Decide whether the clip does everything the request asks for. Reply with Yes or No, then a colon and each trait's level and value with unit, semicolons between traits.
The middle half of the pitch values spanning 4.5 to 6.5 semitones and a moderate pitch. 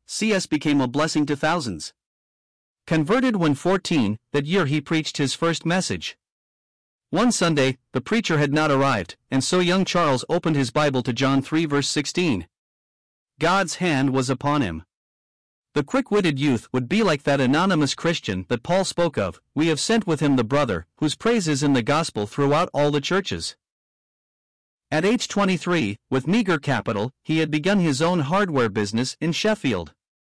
Yes: average, 5.1 semitones; medium, 150 Hz